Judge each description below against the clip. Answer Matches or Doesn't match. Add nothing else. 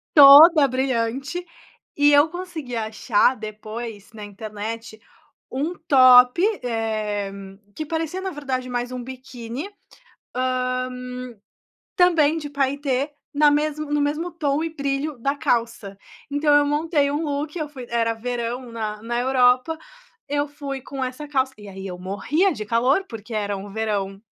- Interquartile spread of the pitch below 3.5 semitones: Doesn't match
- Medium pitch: Doesn't match